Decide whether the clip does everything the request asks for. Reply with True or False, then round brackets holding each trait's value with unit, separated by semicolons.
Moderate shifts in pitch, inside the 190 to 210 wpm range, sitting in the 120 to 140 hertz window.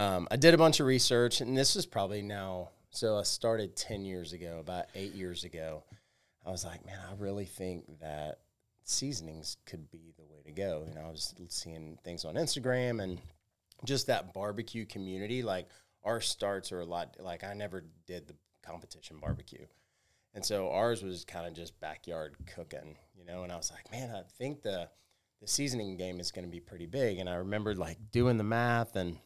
False (4.7 semitones; 200 wpm; 95 Hz)